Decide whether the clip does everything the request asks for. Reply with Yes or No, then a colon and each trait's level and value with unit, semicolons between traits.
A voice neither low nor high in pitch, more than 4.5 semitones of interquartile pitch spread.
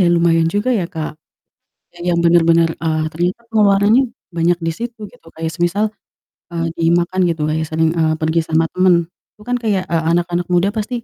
No: medium, 170 Hz; average, 2.7 semitones